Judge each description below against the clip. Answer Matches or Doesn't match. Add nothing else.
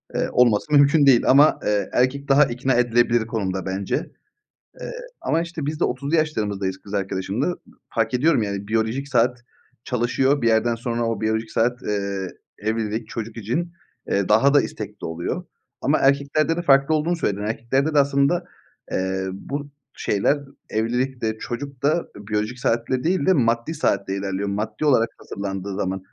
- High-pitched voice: Doesn't match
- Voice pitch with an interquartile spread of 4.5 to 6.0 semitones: Matches